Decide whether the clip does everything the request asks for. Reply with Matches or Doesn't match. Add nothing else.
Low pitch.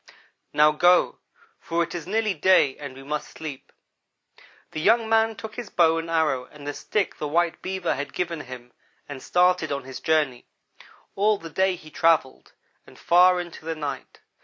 Doesn't match